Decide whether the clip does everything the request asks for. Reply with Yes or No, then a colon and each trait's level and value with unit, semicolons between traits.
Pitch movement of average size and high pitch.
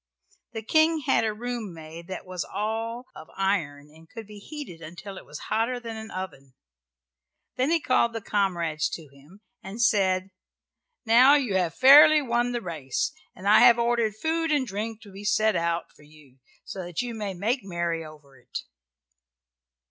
No: wide, 5.8 semitones; high, 205 Hz